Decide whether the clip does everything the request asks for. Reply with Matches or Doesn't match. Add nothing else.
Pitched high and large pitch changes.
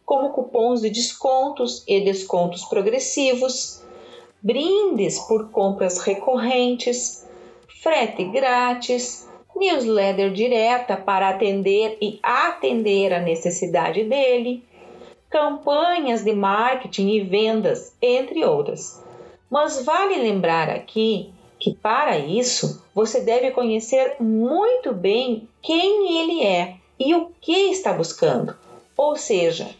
Matches